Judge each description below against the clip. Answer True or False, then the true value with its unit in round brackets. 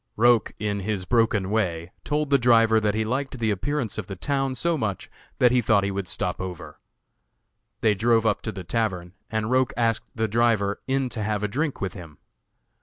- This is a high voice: False (110 Hz)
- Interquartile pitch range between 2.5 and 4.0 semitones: True (3.6 semitones)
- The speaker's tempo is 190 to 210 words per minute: True (200 wpm)